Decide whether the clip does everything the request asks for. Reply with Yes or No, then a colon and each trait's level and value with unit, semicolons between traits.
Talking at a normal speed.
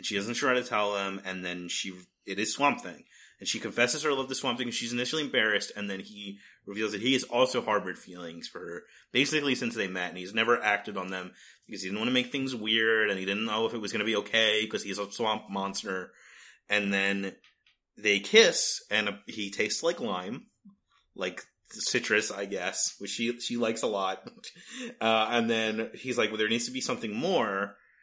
No: fast, 220 wpm